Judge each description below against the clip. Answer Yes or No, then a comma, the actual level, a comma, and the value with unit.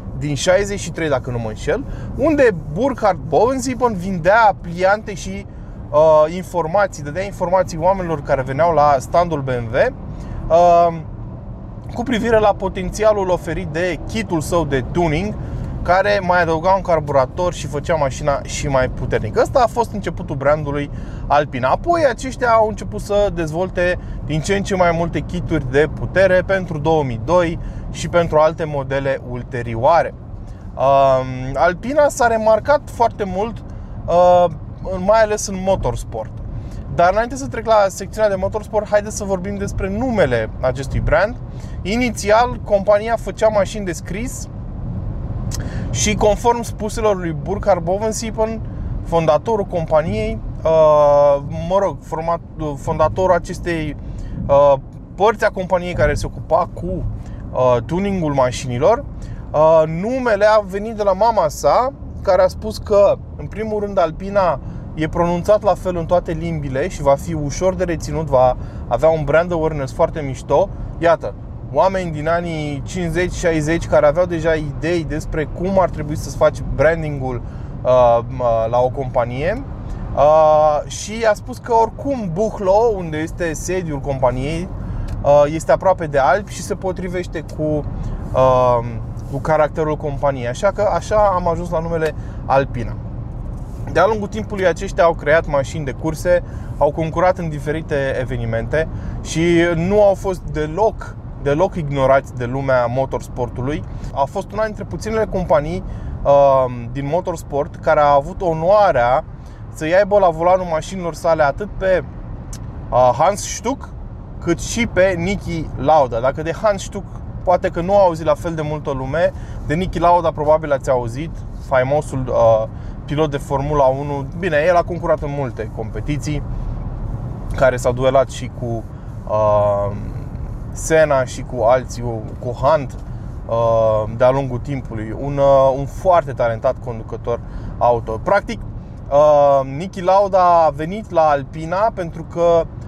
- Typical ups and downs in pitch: No, wide, 6.2 semitones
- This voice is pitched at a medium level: Yes, medium, 150 Hz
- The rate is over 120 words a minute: Yes, average, 135 wpm